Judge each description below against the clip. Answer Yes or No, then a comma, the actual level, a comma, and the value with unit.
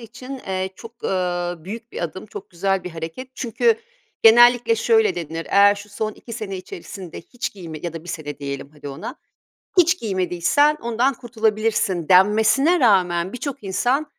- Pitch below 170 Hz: No, high, 205 Hz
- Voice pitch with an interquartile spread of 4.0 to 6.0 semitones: Yes, wide, 5.5 semitones